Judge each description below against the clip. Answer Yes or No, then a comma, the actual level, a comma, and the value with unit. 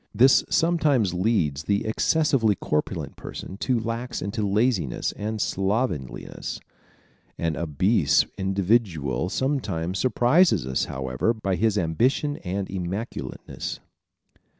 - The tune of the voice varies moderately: No, wide, 5.7 semitones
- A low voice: Yes, low, 100 Hz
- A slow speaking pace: Yes, slow, 105 wpm